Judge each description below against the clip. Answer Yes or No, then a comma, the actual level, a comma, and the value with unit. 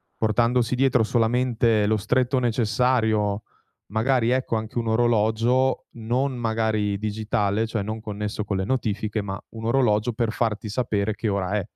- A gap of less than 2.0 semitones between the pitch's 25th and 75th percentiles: No, narrow, 2.4 semitones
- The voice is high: No, low, 110 Hz